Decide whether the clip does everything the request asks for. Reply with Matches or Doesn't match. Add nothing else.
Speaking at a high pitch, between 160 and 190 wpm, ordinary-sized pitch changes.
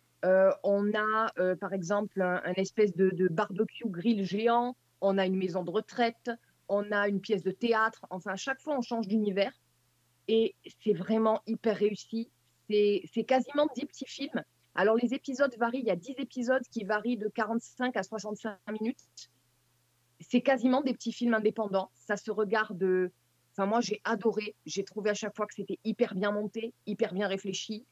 Matches